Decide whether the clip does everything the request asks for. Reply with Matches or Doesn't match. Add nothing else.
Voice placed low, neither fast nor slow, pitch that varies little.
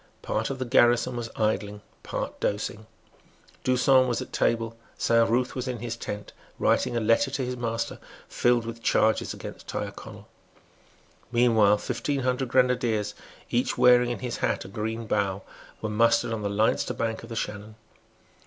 Matches